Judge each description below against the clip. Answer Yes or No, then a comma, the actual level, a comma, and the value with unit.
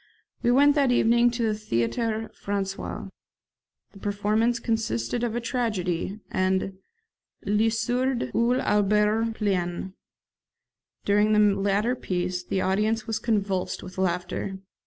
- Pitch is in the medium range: No, high, 210 Hz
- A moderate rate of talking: No, slow, 120 wpm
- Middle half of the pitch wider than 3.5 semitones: No, average, 3.2 semitones